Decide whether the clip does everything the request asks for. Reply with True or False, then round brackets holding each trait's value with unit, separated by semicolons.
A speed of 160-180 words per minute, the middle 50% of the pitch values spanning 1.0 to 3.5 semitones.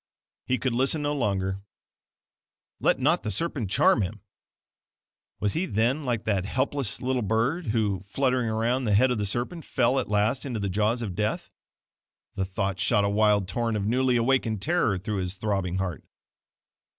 False (175 wpm; 4.3 semitones)